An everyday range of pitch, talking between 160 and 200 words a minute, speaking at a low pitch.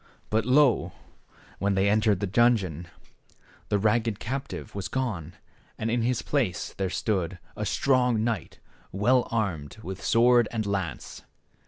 No: average, 3.8 semitones; average, 140 wpm; low, 110 Hz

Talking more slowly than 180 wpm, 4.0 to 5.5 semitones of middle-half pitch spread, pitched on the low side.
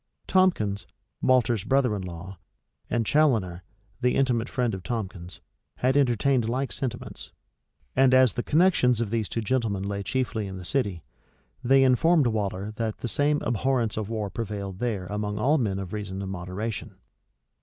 Yes: average, 160 wpm; average, 4.5 semitones; low, 115 Hz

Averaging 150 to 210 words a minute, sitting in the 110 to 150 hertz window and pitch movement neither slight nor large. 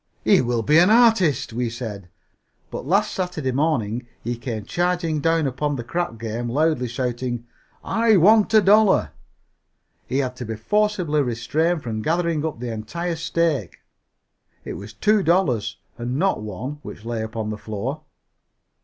No: average, 155 wpm; medium, 140 Hz; wide, 6.6 semitones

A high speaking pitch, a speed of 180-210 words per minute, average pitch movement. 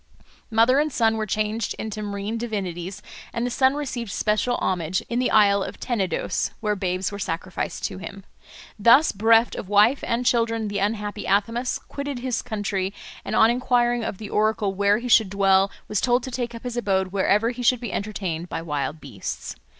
Yes: high, 215 Hz; average, 190 wpm; average, 3.4 semitones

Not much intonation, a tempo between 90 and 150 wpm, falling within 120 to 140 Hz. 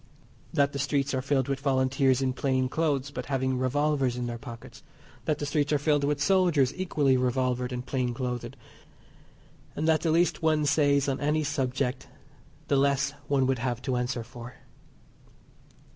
No: narrow, 2.2 semitones; average, 170 wpm; low, 135 Hz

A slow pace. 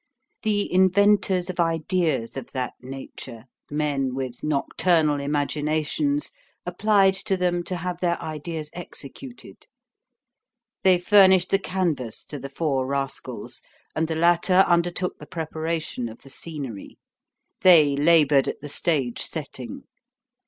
Yes: slow, 125 wpm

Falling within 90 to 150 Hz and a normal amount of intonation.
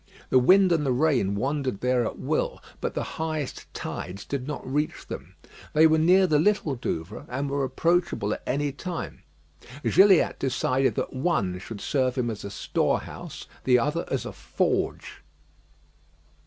Yes: medium, 140 Hz; average, 4.1 semitones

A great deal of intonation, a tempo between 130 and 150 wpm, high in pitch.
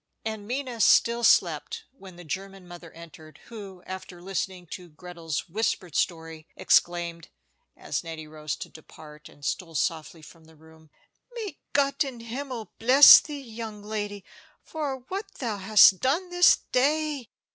Yes: wide, 7.1 semitones; average, 145 wpm; high, 195 Hz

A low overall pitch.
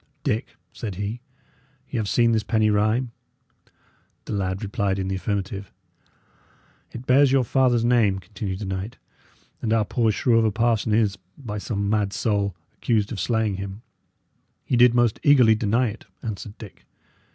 Yes: low, 110 Hz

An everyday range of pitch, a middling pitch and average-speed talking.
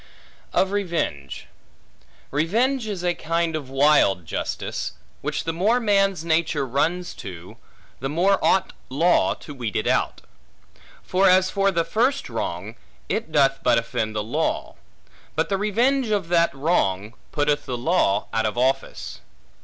No: wide, 6.9 semitones; medium, 165 Hz; average, 145 wpm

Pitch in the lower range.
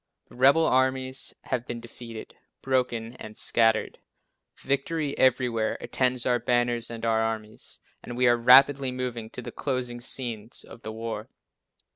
Yes: low, 120 Hz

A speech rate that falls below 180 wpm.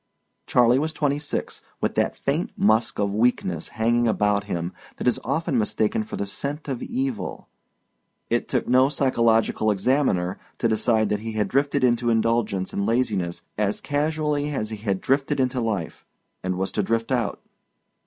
Yes: average, 165 wpm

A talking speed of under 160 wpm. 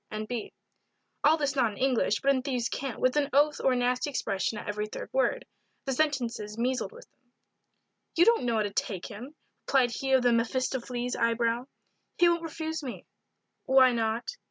No: average, 195 wpm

